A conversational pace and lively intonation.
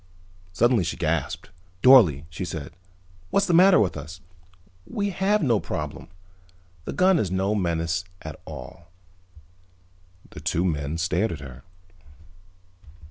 No: slow, 130 wpm; wide, 8.1 semitones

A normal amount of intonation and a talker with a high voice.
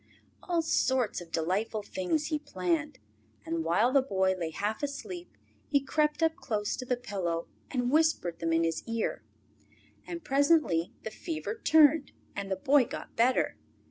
No: wide, 8.4 semitones; high, 240 Hz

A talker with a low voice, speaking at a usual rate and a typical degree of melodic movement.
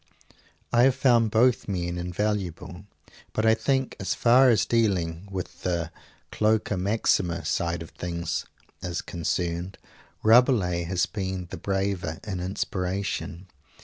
No: very low, 95 Hz; slow, 130 wpm; average, 4.0 semitones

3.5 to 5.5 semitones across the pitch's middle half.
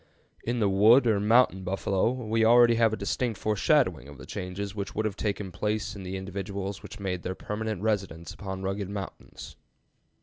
No: narrow, 2.5 semitones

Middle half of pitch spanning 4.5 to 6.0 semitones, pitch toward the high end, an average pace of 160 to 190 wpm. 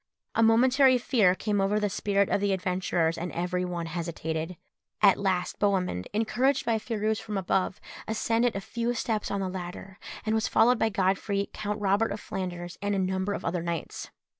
No: average, 3.3 semitones; high, 200 Hz; average, 185 wpm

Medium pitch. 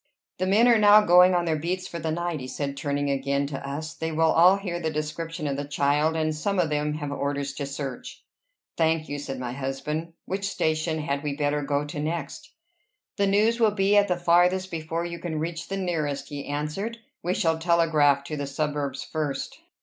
Yes: medium, 155 Hz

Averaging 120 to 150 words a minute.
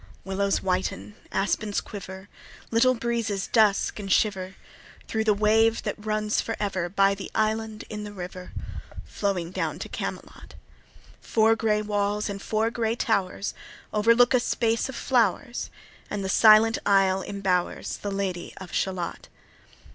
Yes: average, 140 wpm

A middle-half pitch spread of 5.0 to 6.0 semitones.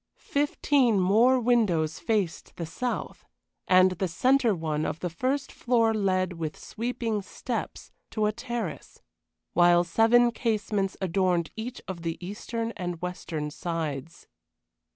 Yes: average, 5.3 semitones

